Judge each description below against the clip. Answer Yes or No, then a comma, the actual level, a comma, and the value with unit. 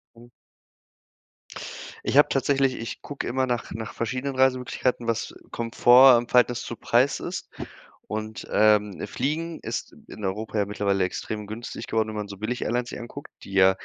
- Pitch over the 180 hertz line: No, low, 115 Hz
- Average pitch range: Yes, average, 3.2 semitones